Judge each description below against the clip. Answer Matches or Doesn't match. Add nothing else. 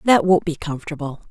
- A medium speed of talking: Matches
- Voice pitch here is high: Doesn't match